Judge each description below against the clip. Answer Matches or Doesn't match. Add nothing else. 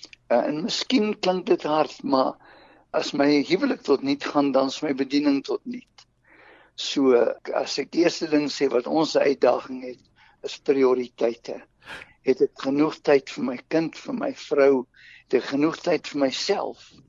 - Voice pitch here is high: Doesn't match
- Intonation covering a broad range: Matches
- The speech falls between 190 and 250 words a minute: Doesn't match